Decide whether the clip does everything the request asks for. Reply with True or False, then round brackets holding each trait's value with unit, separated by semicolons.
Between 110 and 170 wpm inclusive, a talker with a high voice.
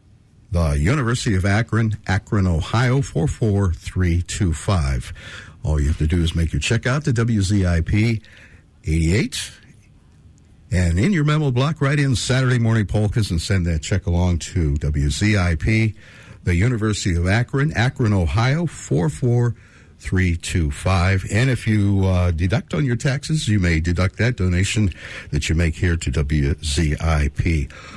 False (155 wpm; 100 Hz)